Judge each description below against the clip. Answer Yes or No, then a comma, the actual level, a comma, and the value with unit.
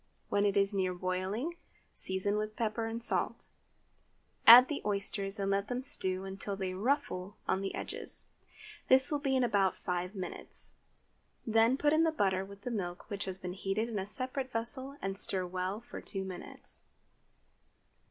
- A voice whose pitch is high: Yes, high, 200 Hz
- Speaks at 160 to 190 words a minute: Yes, average, 170 wpm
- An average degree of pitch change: Yes, average, 3.8 semitones